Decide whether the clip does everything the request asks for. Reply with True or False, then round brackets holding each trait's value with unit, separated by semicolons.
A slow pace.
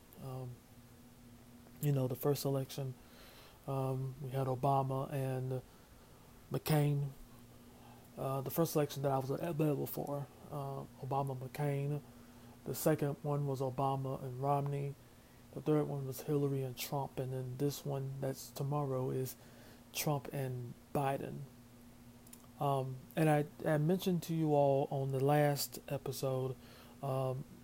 True (130 wpm)